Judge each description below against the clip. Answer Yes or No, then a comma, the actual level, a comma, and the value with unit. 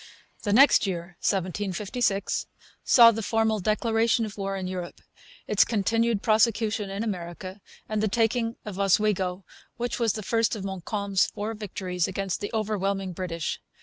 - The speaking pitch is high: Yes, high, 205 Hz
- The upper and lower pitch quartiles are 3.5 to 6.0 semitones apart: No, average, 2.7 semitones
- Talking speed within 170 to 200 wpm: No, average, 150 wpm